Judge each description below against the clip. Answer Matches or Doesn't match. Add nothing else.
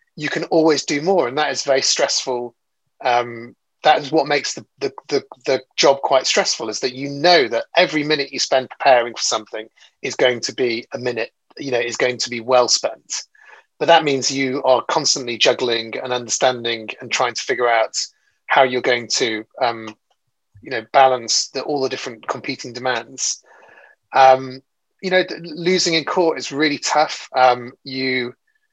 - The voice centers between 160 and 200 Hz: Doesn't match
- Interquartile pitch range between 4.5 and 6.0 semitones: Doesn't match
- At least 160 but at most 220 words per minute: Matches